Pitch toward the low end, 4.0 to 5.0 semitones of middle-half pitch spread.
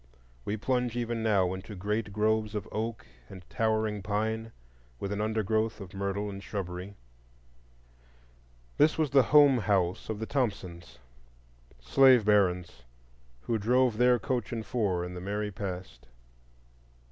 No: low, 105 Hz; average, 3.3 semitones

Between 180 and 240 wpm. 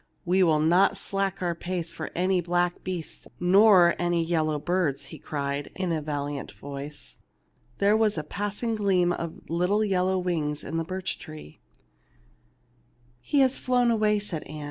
No: average, 160 wpm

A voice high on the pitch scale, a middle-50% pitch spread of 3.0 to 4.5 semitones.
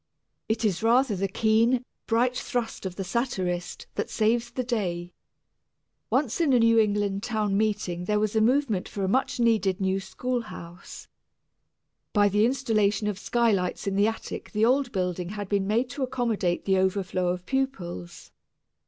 Yes: high, 215 Hz; average, 3.8 semitones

